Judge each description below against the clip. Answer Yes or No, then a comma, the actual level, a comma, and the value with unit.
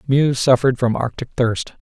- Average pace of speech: Yes, average, 160 wpm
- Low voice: Yes, low, 125 Hz